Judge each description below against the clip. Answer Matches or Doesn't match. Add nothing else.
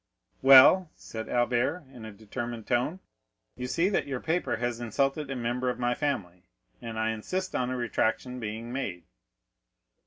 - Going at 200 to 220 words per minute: Doesn't match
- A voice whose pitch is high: Doesn't match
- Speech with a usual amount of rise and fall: Matches